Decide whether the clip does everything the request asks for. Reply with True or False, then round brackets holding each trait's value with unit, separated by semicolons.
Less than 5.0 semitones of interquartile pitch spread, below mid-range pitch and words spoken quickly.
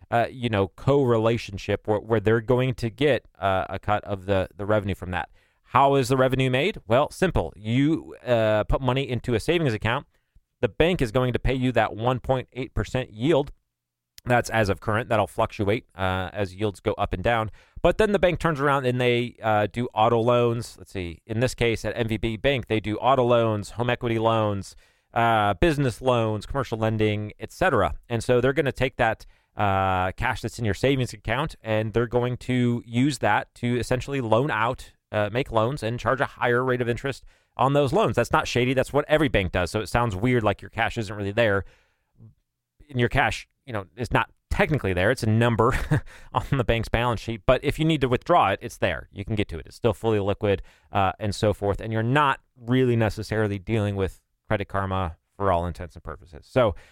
True (3.4 semitones; 115 Hz; 210 wpm)